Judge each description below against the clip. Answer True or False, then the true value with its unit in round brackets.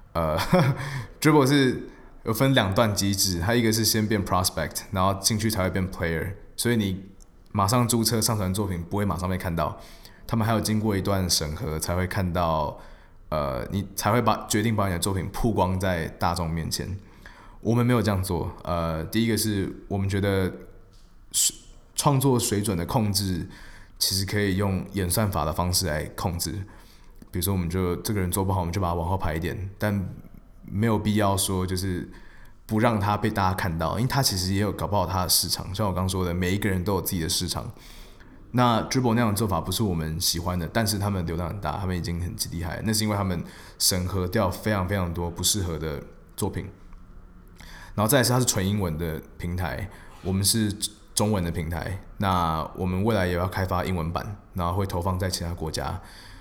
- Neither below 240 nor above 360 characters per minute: True (310 characters per minute)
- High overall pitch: False (95 Hz)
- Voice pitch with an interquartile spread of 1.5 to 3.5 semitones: True (3.2 semitones)